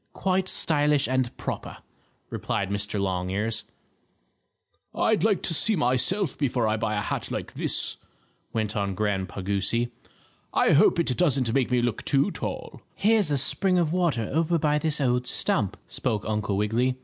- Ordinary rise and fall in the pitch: No, wide, 6.9 semitones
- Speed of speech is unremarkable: Yes, average, 160 wpm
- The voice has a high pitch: No, low, 125 Hz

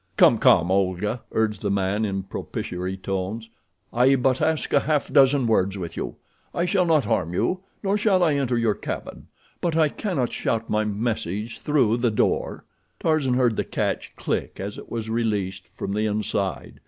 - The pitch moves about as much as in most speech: No, wide, 5.7 semitones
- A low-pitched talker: Yes, low, 115 Hz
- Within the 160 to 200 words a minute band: Yes, average, 180 wpm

